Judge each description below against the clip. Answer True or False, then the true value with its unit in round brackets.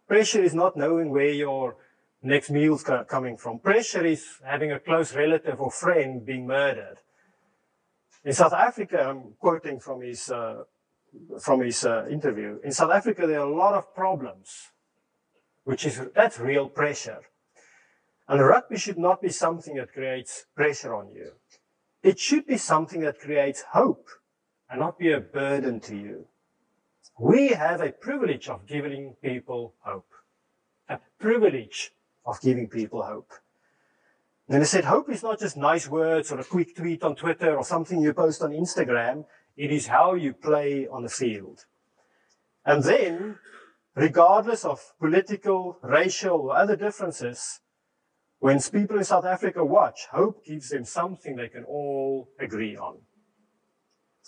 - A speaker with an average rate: True (155 wpm)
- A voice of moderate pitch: True (150 Hz)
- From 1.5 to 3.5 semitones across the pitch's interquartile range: False (4.8 semitones)